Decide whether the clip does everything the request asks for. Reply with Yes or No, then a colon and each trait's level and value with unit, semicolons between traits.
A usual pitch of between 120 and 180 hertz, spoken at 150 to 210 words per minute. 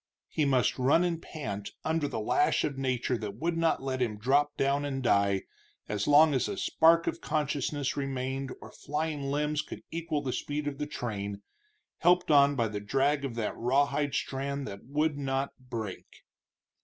Yes: medium, 140 Hz; average, 180 wpm